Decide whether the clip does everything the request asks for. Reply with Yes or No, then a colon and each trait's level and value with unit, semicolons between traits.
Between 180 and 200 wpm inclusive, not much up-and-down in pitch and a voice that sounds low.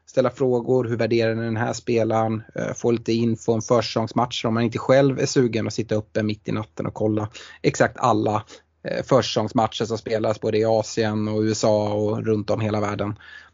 Yes: average, 190 wpm; narrow, 1.7 semitones; low, 110 Hz